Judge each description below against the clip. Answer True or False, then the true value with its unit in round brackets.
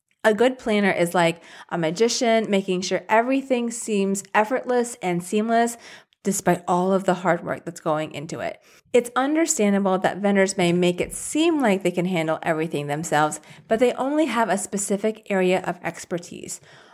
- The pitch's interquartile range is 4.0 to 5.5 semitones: True (4.7 semitones)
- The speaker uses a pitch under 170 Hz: False (190 Hz)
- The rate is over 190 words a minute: False (165 wpm)